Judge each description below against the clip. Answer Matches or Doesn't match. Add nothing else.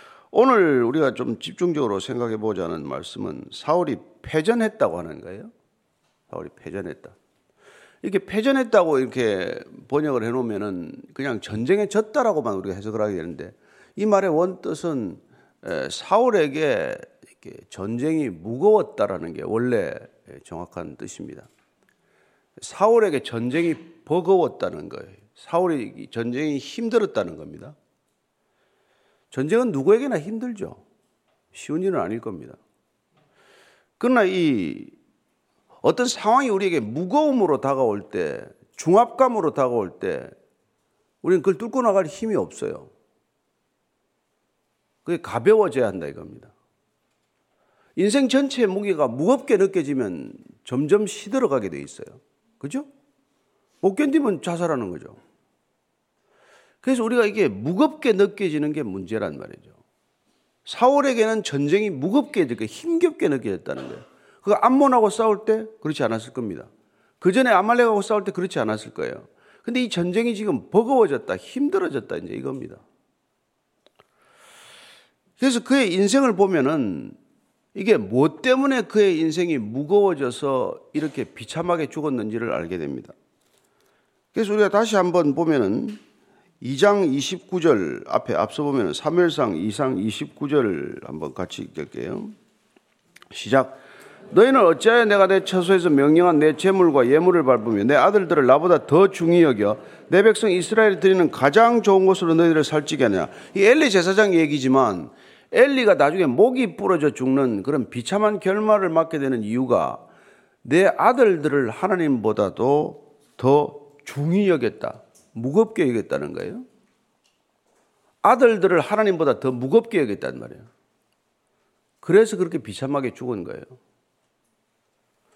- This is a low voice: Doesn't match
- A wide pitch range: Matches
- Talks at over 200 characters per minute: Matches